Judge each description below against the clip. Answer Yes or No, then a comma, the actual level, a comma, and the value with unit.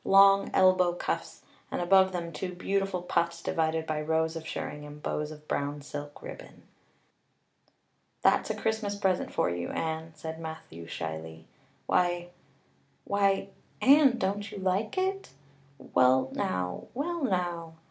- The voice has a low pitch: No, medium, 170 Hz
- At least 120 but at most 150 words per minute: Yes, slow, 135 wpm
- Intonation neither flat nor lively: Yes, average, 4.4 semitones